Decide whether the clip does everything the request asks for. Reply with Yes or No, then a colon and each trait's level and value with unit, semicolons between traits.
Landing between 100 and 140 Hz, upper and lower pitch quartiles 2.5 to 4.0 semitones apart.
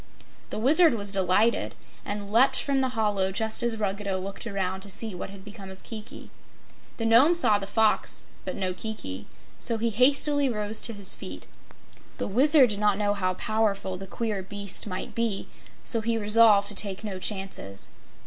No: high, 210 Hz; average, 2.8 semitones